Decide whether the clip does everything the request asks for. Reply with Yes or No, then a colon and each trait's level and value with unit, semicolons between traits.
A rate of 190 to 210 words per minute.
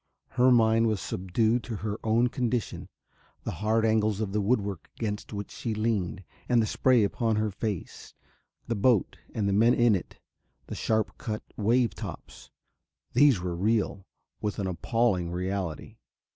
No: average, 160 wpm